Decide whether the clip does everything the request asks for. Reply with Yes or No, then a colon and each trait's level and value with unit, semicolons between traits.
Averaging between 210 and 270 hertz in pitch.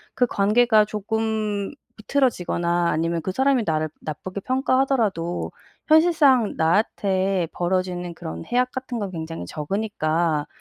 No: high, 200 Hz